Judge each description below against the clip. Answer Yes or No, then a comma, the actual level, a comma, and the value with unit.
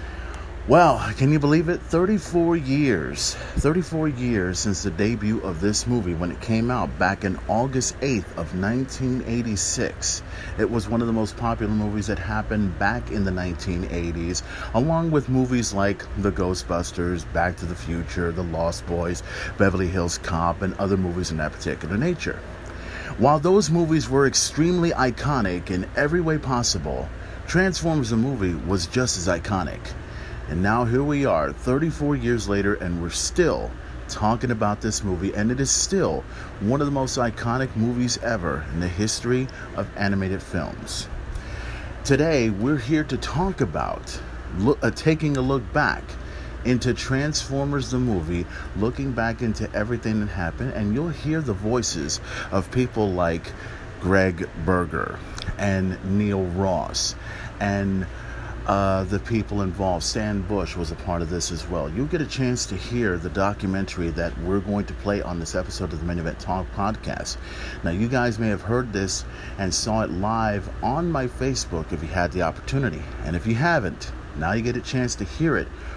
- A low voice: Yes, low, 100 Hz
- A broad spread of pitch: Yes, wide, 5.7 semitones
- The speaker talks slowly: No, average, 170 wpm